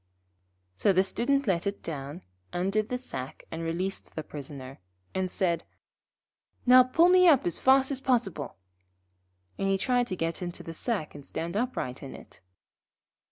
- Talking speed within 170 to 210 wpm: No, average, 160 wpm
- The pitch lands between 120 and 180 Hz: No, high, 190 Hz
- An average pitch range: No, wide, 7.3 semitones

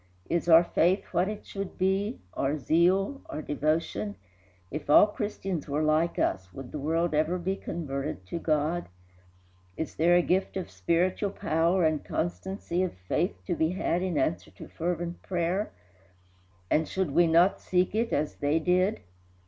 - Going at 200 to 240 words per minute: No, average, 165 wpm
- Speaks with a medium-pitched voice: Yes, medium, 170 Hz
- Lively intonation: No, average, 3.3 semitones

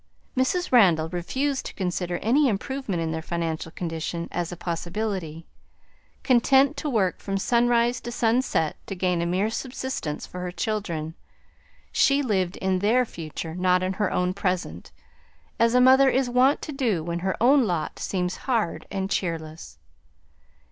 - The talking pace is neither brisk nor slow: Yes, average, 155 wpm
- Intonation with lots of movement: Yes, wide, 6.2 semitones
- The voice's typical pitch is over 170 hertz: Yes, high, 190 Hz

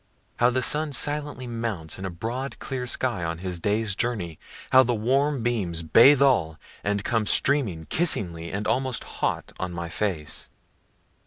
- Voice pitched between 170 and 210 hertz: No, low, 115 Hz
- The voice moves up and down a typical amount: No, wide, 6.6 semitones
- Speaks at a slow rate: No, average, 160 wpm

